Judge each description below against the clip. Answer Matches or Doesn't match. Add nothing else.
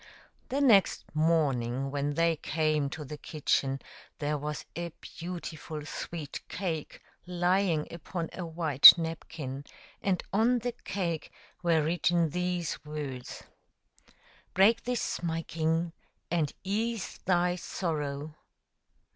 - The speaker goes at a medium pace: Doesn't match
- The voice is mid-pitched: Matches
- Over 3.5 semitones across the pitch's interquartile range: Doesn't match